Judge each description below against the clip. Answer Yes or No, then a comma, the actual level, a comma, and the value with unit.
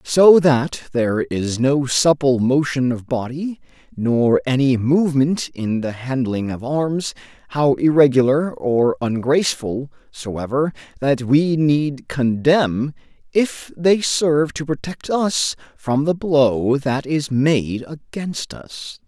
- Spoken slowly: Yes, slow, 125 wpm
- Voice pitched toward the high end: No, medium, 140 Hz